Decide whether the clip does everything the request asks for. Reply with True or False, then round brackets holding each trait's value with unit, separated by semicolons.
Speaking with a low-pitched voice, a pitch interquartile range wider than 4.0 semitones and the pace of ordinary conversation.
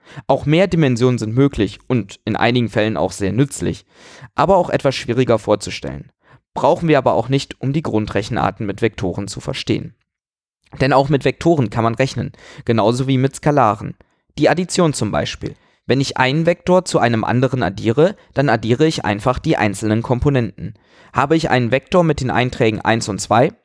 True (125 Hz; 4.8 semitones; 175 wpm)